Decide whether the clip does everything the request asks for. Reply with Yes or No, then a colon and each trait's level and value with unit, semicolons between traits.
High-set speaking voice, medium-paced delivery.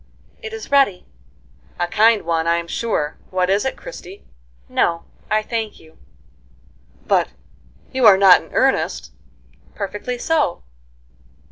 No: high, 200 Hz; slow, 125 wpm